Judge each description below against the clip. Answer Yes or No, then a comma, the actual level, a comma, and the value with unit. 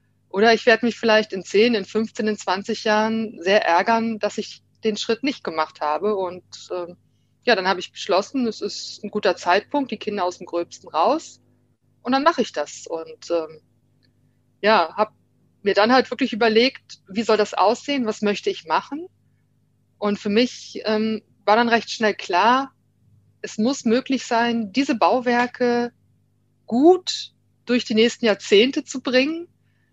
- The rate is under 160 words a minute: No, average, 165 wpm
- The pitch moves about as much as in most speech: Yes, average, 3.4 semitones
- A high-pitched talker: Yes, high, 220 Hz